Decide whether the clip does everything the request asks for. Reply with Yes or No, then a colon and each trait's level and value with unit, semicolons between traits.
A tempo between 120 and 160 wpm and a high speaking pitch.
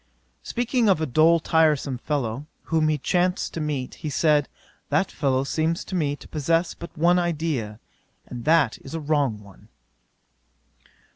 No: average, 155 wpm; medium, 155 Hz